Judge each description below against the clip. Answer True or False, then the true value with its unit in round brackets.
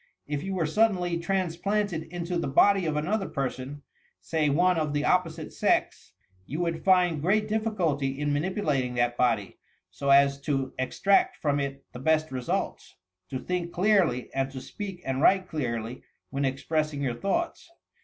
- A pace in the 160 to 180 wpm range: True (165 wpm)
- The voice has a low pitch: False (155 Hz)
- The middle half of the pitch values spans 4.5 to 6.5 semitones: True (5.1 semitones)